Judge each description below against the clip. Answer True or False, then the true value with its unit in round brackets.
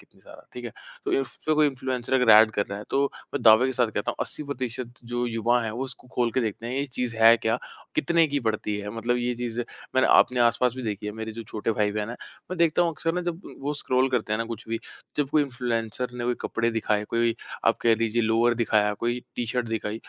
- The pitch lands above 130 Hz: False (120 Hz)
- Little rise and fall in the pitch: True (2.3 semitones)